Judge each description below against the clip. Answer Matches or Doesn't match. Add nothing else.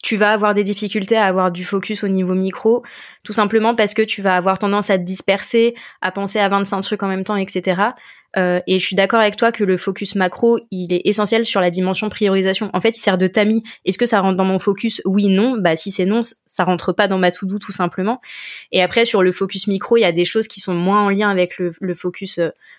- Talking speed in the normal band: Doesn't match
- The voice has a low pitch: Doesn't match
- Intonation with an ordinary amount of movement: Doesn't match